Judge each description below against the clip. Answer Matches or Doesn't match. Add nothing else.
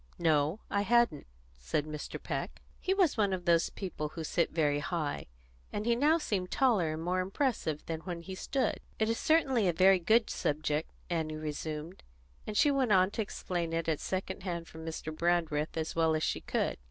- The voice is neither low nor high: Matches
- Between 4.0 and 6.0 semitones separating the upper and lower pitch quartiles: Matches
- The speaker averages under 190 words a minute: Doesn't match